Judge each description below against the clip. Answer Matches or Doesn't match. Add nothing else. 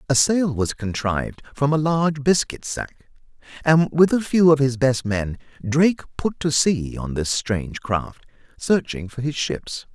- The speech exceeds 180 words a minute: Doesn't match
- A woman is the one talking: Doesn't match